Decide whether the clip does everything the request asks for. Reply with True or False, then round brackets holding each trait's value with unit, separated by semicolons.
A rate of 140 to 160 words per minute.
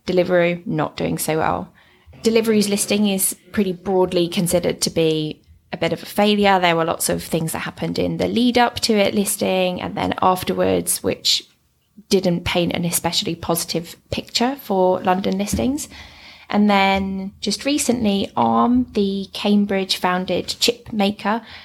True (150 wpm)